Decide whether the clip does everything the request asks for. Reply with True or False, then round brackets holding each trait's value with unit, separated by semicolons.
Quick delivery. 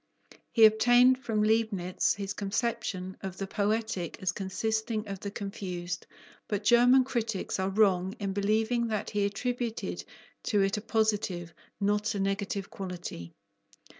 False (135 wpm)